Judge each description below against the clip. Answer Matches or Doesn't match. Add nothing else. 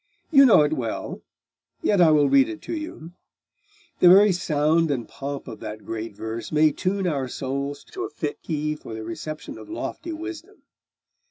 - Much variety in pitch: Matches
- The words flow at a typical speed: Matches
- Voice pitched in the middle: Matches